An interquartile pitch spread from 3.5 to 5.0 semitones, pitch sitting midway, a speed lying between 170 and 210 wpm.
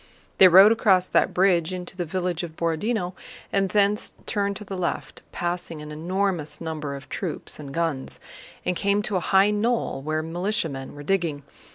Yes: average, 3.8 semitones; medium, 180 Hz; average, 175 wpm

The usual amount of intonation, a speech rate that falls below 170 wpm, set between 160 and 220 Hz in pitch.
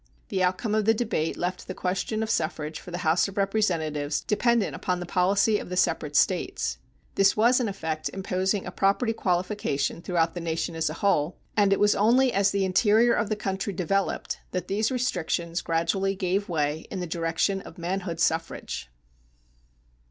No: average, 3.6 semitones; average, 180 wpm; high, 190 Hz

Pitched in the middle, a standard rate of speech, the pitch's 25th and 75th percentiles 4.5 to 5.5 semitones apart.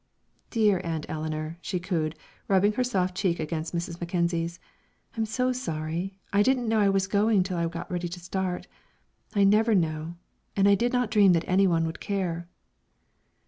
No: medium, 180 Hz; average, 180 wpm; average, 3.4 semitones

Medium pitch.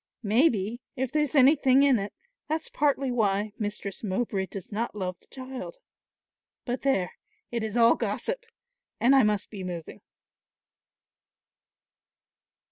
No: high, 235 Hz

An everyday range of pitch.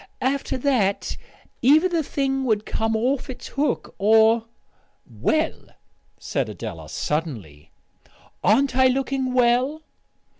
Yes: average, 3.8 semitones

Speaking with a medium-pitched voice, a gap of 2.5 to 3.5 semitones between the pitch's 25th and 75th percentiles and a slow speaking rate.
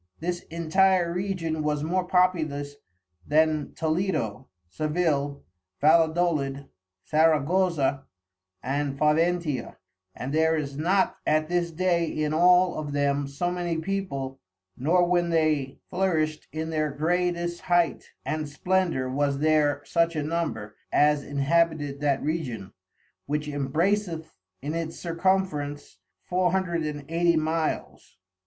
Yes: medium, 155 Hz; average, 3.1 semitones; slow, 120 wpm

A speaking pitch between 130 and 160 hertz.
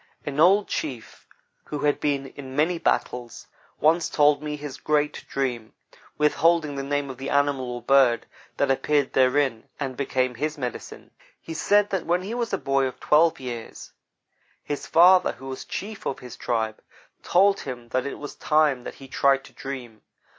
Yes: medium, 140 Hz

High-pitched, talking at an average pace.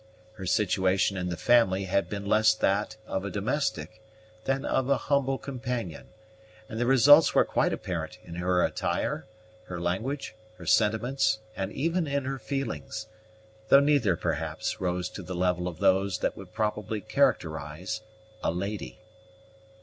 No: low, 105 Hz; average, 150 wpm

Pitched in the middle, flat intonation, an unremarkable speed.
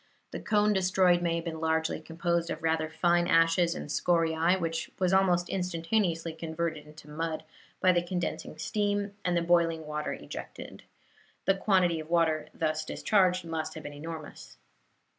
Yes: medium, 170 Hz; narrow, 2.0 semitones; average, 160 wpm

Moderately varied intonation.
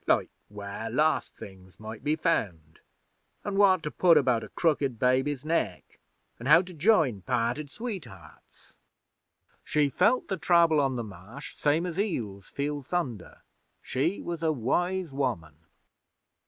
No: wide, 6.9 semitones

